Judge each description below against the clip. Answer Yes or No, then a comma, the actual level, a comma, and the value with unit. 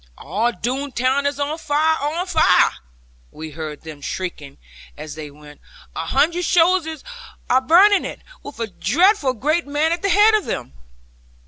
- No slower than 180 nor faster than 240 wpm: No, average, 160 wpm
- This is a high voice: Yes, very high, 285 Hz